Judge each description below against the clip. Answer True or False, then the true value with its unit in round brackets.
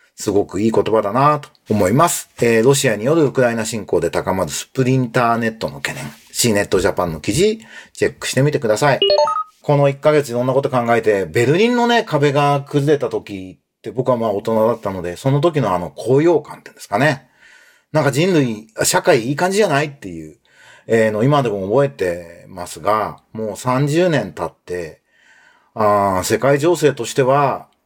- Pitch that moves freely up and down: False (5.0 semitones)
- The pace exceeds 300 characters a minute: True (365 characters per minute)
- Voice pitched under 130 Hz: False (135 Hz)